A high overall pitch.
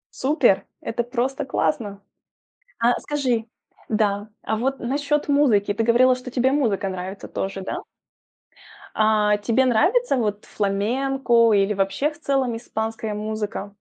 Yes: high, 230 Hz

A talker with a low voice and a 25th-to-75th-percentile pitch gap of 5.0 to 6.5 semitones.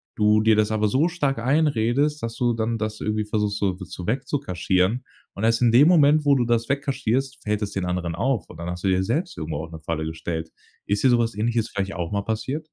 Yes: low, 110 Hz; wide, 5.6 semitones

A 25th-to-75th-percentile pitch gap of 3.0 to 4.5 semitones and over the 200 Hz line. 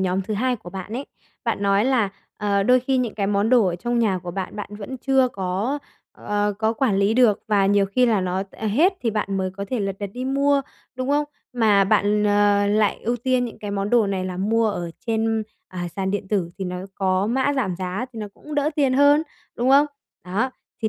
Yes: average, 4.2 semitones; high, 210 Hz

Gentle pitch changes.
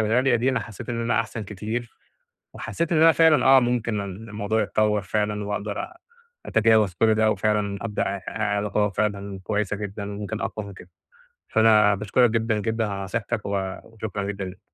Yes: narrow, 1.9 semitones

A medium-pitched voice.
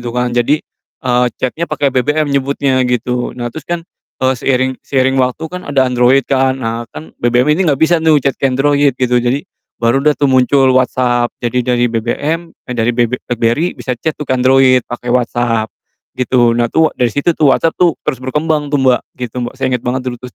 No: low, 130 Hz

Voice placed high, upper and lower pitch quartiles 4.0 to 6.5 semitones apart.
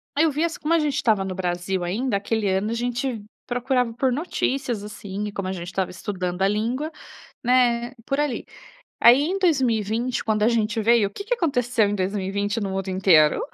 Yes: high, 225 Hz; average, 4.6 semitones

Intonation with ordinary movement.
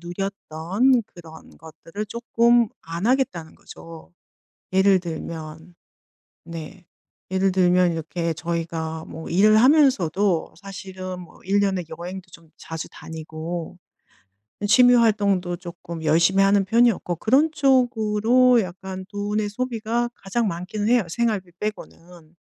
Yes: average, 4.4 semitones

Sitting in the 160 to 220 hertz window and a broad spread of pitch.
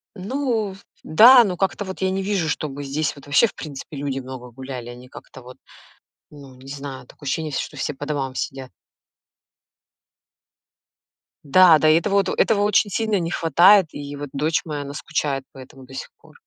No: medium, 150 Hz; wide, 5.7 semitones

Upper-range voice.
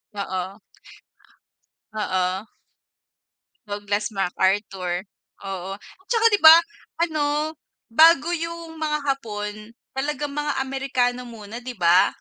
Yes: high, 245 Hz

